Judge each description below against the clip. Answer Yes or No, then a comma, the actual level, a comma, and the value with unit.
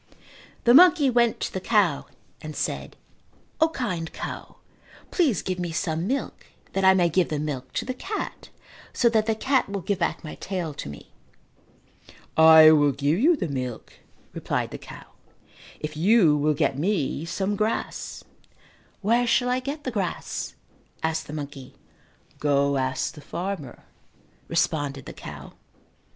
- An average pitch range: No, wide, 7.3 semitones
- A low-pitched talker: No, medium, 175 Hz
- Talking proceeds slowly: No, average, 155 wpm